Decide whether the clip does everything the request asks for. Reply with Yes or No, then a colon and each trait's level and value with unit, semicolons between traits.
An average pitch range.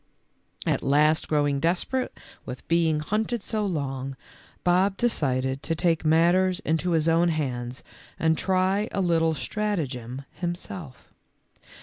Yes: average, 4.5 semitones